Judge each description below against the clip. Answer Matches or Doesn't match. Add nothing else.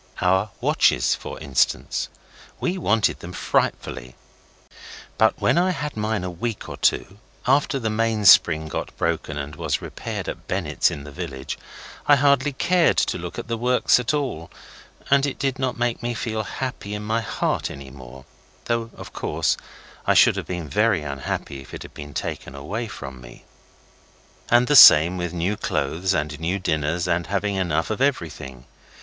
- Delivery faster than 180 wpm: Doesn't match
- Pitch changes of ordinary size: Doesn't match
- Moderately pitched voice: Doesn't match